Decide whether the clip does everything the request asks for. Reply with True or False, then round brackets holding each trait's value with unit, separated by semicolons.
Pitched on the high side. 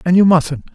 False (165 Hz)